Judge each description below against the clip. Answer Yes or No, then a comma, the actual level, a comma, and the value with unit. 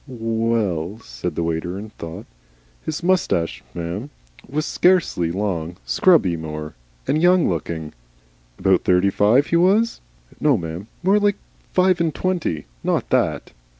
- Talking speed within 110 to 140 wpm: Yes, slow, 135 wpm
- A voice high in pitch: No, low, 105 Hz